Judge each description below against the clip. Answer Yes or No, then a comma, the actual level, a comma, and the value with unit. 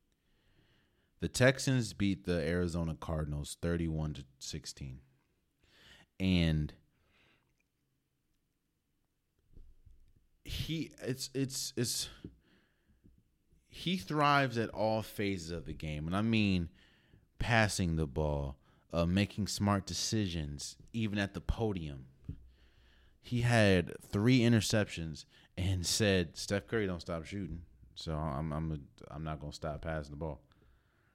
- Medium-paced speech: No, slow, 110 wpm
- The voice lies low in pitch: Yes, very low, 90 Hz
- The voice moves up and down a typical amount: No, wide, 5.8 semitones